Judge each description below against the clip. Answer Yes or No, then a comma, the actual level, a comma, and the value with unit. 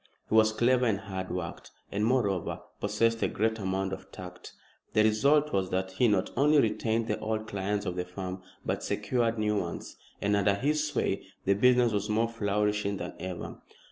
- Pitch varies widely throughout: No, average, 3.1 semitones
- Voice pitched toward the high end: No, low, 105 Hz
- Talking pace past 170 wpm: Yes, average, 185 wpm